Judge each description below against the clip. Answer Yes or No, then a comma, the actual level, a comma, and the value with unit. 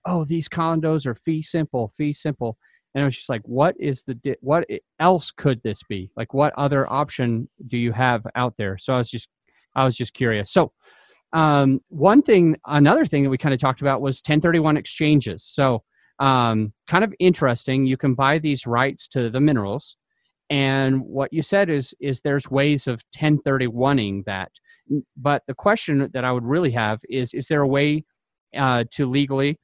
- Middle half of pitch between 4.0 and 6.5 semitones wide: No, average, 3.2 semitones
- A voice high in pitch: No, low, 135 Hz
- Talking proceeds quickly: No, average, 190 wpm